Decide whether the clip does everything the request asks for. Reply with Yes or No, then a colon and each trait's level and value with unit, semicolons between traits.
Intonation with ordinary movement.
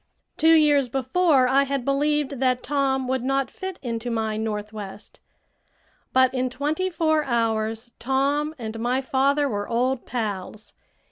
Yes: average, 3.6 semitones